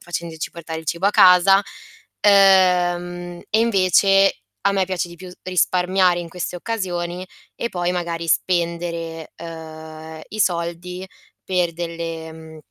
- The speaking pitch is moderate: Yes, medium, 175 Hz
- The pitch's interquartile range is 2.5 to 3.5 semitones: No, narrow, 1.8 semitones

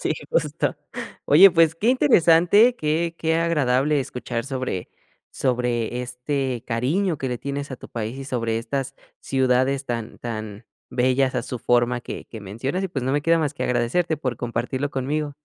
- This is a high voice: No, low, 130 Hz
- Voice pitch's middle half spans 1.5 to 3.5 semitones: No, average, 4.1 semitones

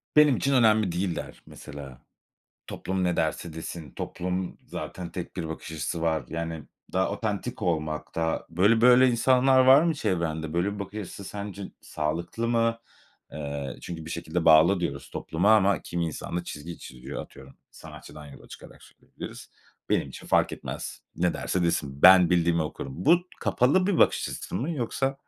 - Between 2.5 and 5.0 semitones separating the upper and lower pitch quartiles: No, wide, 5.5 semitones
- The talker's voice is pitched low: Yes, very low, 90 Hz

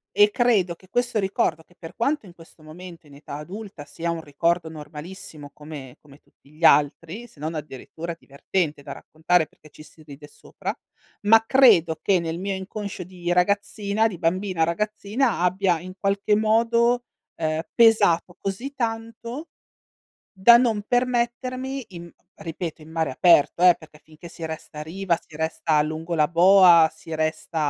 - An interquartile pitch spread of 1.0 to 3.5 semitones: No, average, 4.8 semitones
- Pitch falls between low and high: Yes, medium, 175 Hz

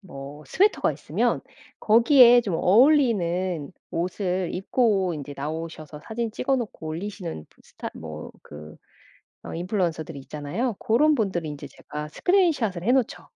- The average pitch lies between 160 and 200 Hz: Yes, medium, 185 Hz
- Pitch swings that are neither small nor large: No, wide, 6.9 semitones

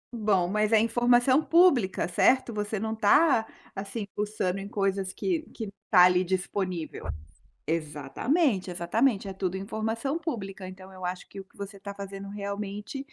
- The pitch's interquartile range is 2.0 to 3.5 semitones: Yes, average, 3.2 semitones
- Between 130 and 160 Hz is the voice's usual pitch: No, high, 200 Hz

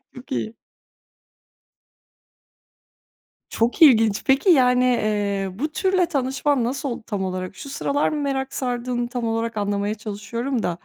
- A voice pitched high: Yes, high, 240 Hz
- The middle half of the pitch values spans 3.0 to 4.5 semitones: Yes, average, 4.2 semitones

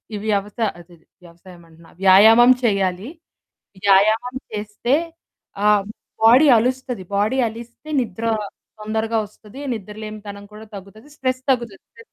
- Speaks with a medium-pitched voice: No, high, 215 Hz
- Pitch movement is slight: No, average, 3.1 semitones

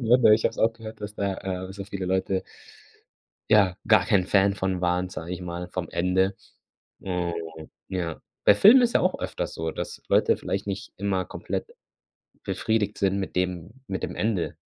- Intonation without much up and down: Yes, narrow, 2.3 semitones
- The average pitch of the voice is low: Yes, very low, 95 Hz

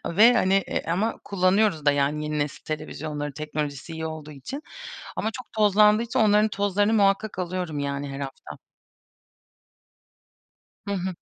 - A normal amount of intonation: No, wide, 5.7 semitones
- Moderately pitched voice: Yes, medium, 180 Hz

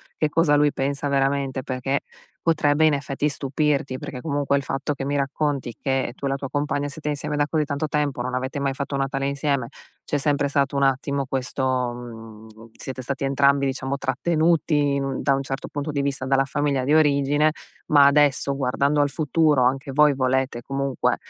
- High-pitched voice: No, medium, 140 Hz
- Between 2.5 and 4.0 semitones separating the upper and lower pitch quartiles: No, narrow, 1.5 semitones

